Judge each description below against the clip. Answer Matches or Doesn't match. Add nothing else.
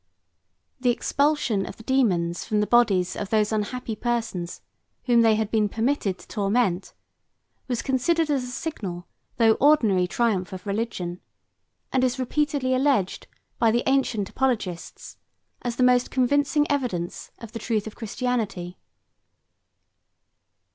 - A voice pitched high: Matches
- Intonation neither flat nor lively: Matches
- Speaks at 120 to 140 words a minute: Matches